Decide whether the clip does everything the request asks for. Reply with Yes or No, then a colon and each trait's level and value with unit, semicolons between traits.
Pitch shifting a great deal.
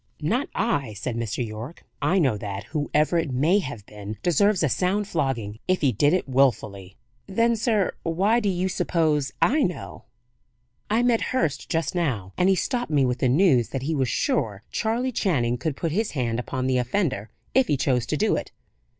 Yes: wide, 7.4 semitones